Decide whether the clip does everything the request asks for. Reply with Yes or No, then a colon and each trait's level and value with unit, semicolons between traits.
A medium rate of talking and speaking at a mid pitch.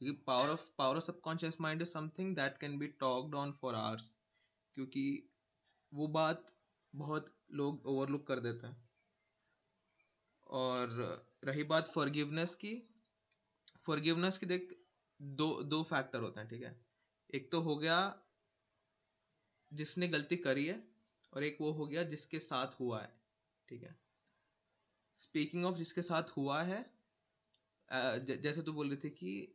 Yes: average, 145 wpm; medium, 145 Hz